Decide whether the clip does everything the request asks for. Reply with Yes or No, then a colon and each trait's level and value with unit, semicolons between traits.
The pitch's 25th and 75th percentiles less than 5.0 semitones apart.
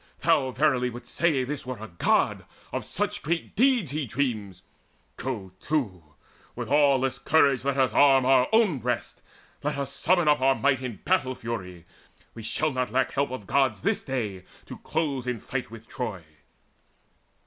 Yes: average, 3.4 semitones